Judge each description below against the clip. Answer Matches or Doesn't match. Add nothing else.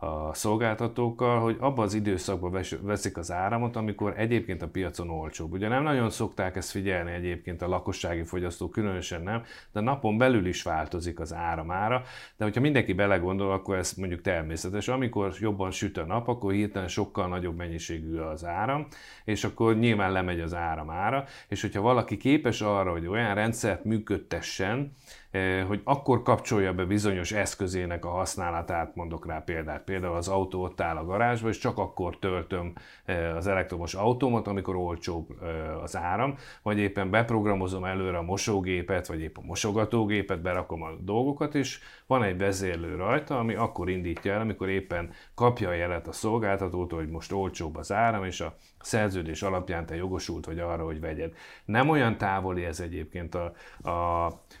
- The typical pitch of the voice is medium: Doesn't match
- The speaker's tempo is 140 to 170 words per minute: Matches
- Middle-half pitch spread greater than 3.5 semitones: Matches